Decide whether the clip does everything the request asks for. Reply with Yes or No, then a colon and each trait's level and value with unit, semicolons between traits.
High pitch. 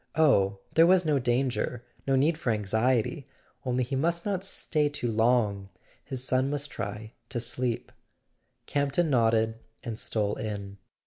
No: low, 125 Hz